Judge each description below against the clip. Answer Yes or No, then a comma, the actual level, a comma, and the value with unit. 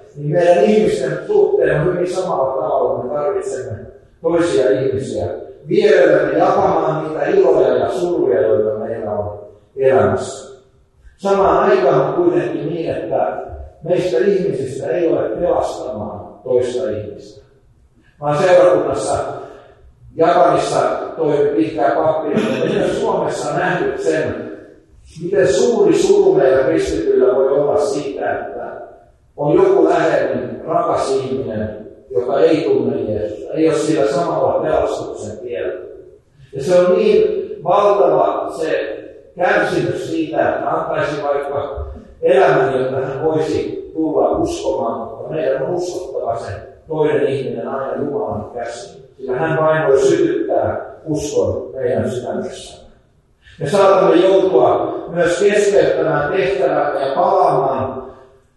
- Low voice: No, medium, 180 Hz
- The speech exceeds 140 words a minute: No, average, 115 wpm